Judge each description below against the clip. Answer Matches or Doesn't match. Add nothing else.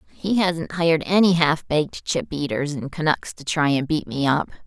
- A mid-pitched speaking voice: Matches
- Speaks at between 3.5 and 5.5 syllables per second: Matches